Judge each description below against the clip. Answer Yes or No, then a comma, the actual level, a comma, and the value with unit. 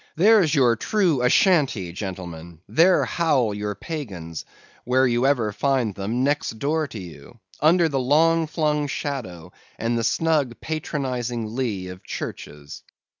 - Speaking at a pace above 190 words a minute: No, slow, 135 wpm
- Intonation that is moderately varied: No, wide, 6.8 semitones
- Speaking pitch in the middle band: No, low, 125 Hz